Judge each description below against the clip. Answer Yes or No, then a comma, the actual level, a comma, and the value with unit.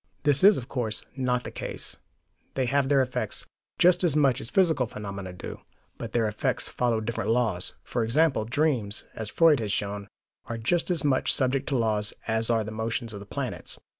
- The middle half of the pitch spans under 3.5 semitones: No, average, 4.3 semitones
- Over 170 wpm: Yes, average, 195 wpm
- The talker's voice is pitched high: No, low, 120 Hz